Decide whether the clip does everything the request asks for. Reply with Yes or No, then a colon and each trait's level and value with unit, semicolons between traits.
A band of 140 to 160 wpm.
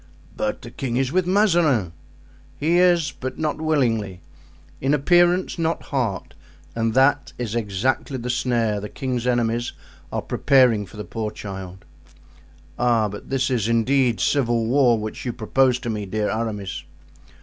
Yes: average, 150 wpm